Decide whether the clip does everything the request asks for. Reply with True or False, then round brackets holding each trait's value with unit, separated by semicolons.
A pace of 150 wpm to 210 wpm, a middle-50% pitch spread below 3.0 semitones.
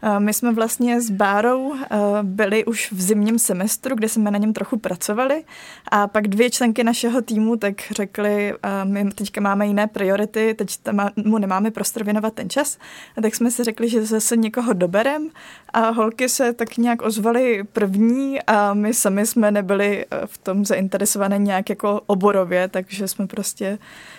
True (165 wpm; 2.5 semitones)